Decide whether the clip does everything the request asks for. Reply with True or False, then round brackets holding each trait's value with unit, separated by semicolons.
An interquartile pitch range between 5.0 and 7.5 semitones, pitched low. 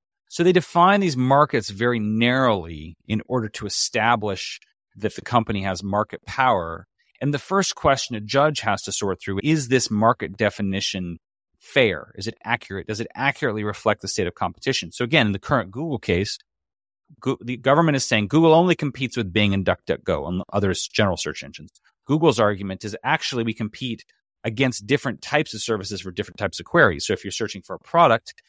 True (5.3 semitones; 115 Hz)